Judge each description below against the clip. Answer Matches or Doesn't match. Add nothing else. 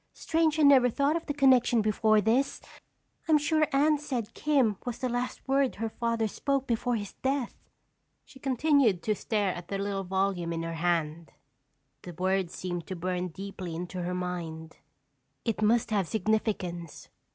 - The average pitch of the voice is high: Matches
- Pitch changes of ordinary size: Doesn't match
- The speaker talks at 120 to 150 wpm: Doesn't match